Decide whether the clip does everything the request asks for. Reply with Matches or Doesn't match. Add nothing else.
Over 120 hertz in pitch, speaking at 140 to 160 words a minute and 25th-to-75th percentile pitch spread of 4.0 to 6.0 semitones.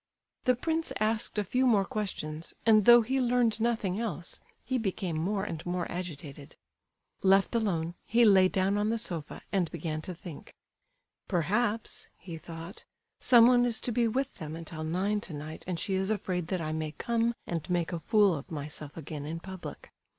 Doesn't match